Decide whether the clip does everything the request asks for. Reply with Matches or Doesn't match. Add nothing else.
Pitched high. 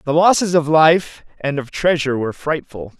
Doesn't match